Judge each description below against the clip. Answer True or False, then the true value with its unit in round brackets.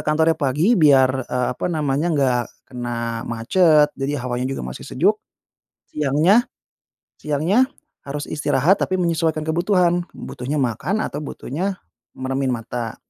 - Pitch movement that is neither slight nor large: True (4.7 semitones)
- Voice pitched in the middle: True (145 Hz)